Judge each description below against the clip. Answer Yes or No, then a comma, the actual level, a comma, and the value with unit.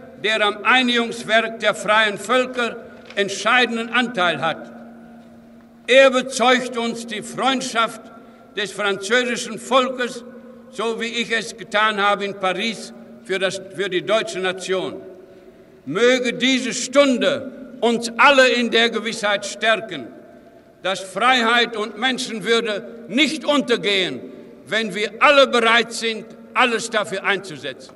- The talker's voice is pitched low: No, high, 230 Hz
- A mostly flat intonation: No, average, 3.1 semitones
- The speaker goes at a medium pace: No, slow, 115 wpm